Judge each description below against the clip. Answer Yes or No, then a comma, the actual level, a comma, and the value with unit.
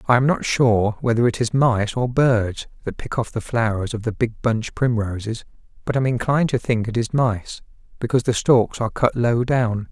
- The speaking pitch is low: Yes, low, 115 Hz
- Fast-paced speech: Yes, fast, 210 wpm